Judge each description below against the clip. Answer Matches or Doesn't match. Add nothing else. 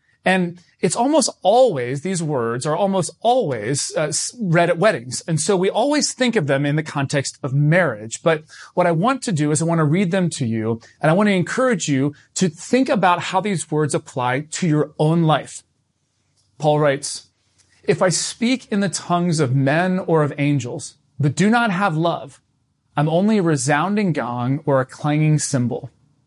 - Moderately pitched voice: Matches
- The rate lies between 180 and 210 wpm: Matches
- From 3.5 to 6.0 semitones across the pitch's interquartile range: Matches